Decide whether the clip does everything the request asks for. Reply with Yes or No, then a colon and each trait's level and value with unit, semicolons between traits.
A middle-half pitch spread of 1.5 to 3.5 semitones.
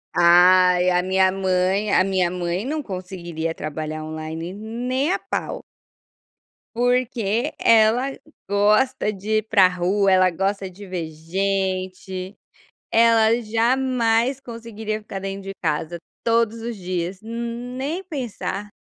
No: average, 4.0 semitones